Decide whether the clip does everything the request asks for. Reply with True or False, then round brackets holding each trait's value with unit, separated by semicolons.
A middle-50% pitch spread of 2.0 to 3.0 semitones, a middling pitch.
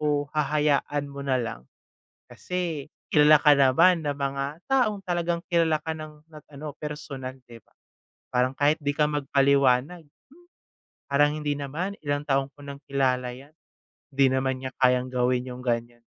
True (2.6 semitones; 145 Hz)